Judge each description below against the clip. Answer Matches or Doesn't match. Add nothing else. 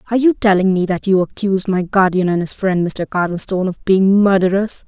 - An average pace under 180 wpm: Doesn't match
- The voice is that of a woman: Matches